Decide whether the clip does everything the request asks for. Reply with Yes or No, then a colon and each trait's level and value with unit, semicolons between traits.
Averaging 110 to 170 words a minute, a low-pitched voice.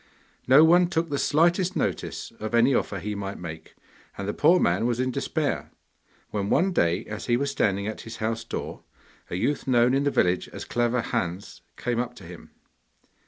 No: average, 195 wpm; low, 120 Hz